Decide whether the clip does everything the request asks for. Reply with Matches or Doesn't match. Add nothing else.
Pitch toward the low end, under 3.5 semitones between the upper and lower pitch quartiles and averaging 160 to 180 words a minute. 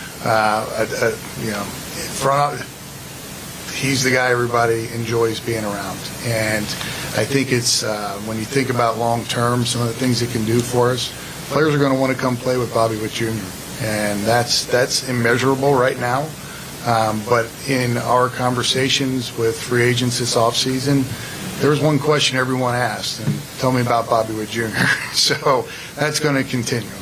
Matches